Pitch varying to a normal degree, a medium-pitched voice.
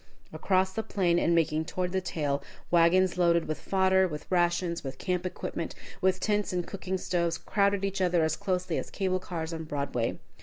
No: narrow, 2.2 semitones; medium, 180 Hz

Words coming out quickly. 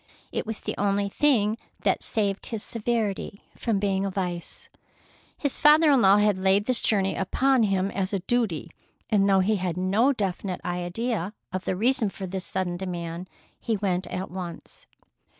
No: average, 170 wpm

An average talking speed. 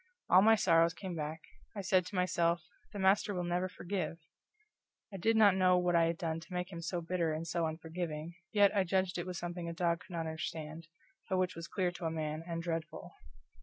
No: fast, 220 wpm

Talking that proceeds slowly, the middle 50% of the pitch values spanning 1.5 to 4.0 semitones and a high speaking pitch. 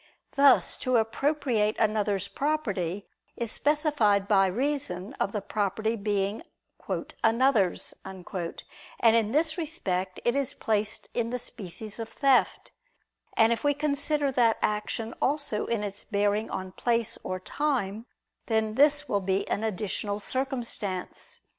No: slow, 130 wpm; average, 4.8 semitones; high, 220 Hz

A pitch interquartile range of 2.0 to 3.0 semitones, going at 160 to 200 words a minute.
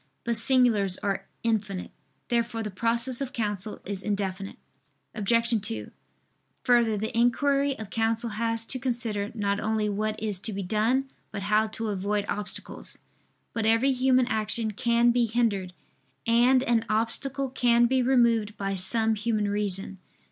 No: narrow, 2.5 semitones; average, 150 wpm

